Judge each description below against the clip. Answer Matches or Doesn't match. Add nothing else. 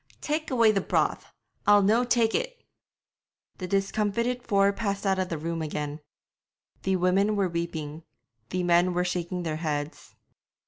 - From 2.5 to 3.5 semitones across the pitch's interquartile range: Doesn't match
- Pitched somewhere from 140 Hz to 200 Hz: Matches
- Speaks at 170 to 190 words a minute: Doesn't match